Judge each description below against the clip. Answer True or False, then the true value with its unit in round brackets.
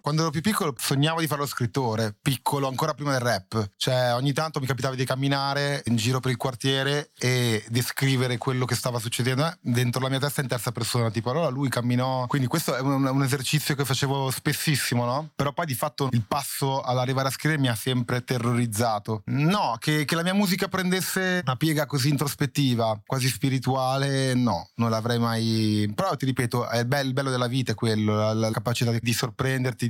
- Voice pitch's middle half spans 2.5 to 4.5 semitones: True (2.9 semitones)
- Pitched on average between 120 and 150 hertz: True (130 Hz)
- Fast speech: True (200 wpm)